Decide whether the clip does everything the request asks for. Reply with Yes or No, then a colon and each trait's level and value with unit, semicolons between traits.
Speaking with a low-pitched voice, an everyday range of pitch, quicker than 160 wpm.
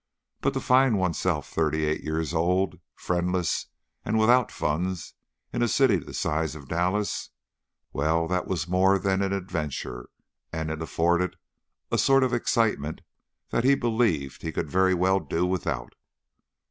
No: very low, 90 Hz; average, 3.6 semitones; average, 150 wpm